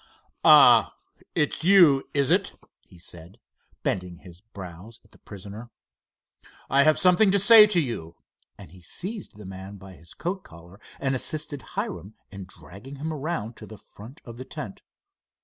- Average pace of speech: Yes, average, 165 wpm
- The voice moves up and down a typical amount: No, wide, 8.7 semitones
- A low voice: Yes, low, 115 Hz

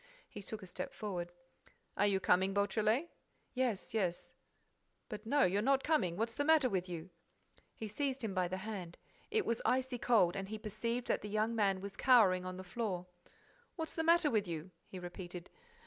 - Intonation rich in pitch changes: No, average, 4.8 semitones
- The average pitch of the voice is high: Yes, high, 210 Hz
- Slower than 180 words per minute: No, average, 185 wpm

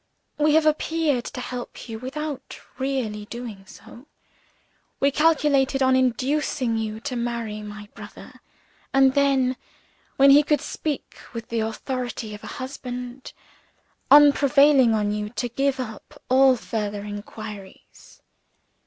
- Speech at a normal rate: No, slow, 130 wpm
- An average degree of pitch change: Yes, average, 4.0 semitones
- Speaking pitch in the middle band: No, very high, 255 Hz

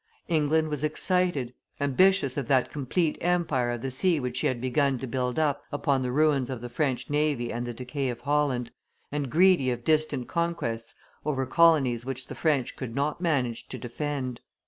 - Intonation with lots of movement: No, average, 3.5 semitones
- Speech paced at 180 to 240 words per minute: Yes, average, 185 wpm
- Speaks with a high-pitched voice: No, medium, 140 Hz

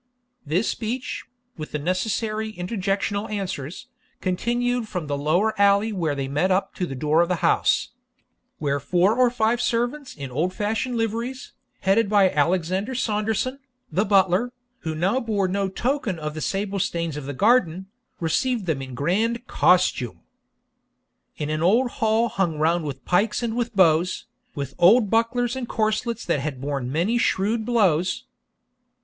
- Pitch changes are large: Yes, wide, 5.8 semitones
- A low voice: No, high, 195 Hz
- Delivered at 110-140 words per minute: No, average, 155 wpm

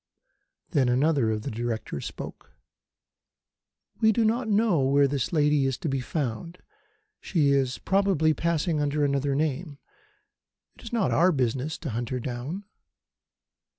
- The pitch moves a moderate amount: Yes, average, 4.5 semitones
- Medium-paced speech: Yes, average, 145 wpm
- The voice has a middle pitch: Yes, medium, 145 Hz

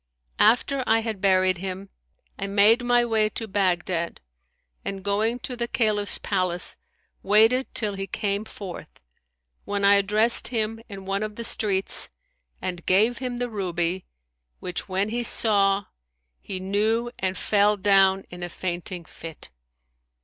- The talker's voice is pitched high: Yes, high, 200 Hz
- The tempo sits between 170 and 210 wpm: No, average, 145 wpm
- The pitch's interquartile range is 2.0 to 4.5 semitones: Yes, average, 2.8 semitones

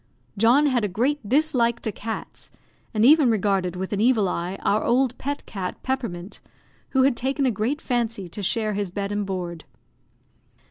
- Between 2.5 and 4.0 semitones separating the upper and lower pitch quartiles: No, average, 4.7 semitones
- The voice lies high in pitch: Yes, high, 220 Hz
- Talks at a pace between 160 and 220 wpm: Yes, average, 175 wpm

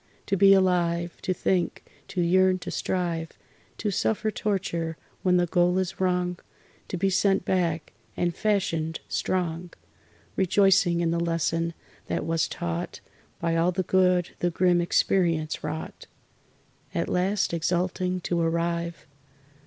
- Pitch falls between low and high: Yes, medium, 175 Hz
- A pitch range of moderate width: No, narrow, 1.8 semitones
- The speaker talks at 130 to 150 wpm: Yes, slow, 135 wpm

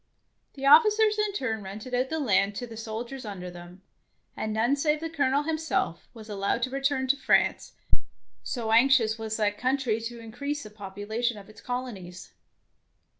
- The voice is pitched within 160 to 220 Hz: No, high, 235 Hz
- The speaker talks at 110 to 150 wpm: No, average, 170 wpm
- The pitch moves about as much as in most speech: Yes, average, 4.4 semitones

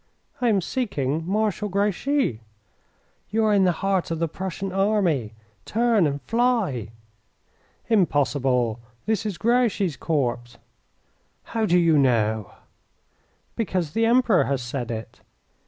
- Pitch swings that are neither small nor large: No, wide, 7.9 semitones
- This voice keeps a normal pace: No, slow, 120 wpm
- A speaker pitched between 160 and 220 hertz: Yes, medium, 185 Hz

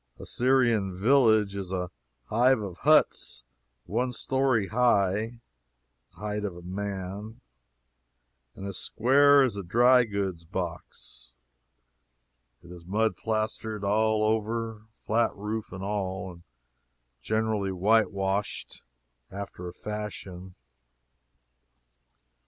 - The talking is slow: Yes, slow, 105 wpm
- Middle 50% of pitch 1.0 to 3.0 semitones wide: Yes, average, 2.7 semitones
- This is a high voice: No, low, 105 Hz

